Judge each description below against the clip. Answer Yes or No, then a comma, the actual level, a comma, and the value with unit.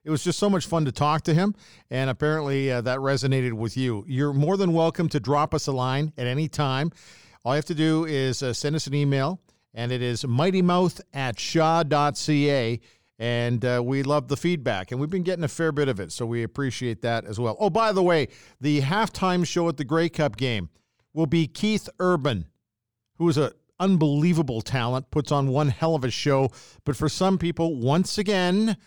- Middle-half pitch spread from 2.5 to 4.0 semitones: No, average, 4.6 semitones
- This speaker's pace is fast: Yes, fast, 210 wpm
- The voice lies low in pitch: No, medium, 145 Hz